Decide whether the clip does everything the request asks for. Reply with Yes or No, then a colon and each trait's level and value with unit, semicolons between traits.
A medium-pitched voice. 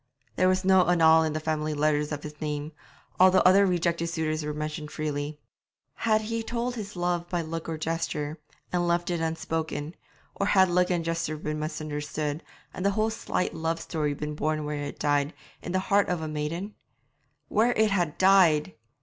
Yes: medium, 165 Hz